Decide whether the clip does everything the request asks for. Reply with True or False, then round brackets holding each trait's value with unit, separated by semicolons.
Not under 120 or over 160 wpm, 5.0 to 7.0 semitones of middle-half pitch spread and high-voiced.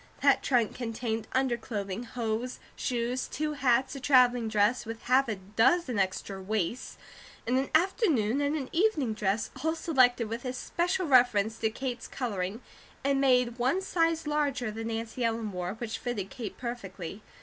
False (155 wpm; 3.5 semitones; 240 Hz)